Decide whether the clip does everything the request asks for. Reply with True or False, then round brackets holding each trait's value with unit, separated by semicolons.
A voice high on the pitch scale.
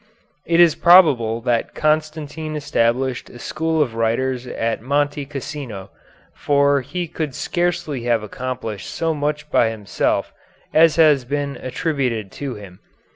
False (140 Hz)